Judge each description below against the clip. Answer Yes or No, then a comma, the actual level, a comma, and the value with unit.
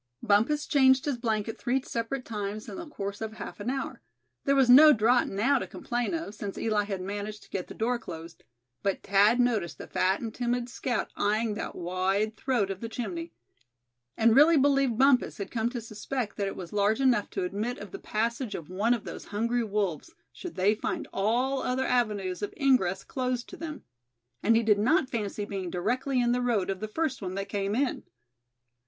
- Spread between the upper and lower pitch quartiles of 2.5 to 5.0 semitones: Yes, average, 3.8 semitones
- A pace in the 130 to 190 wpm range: No, fast, 205 wpm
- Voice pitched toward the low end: No, high, 225 Hz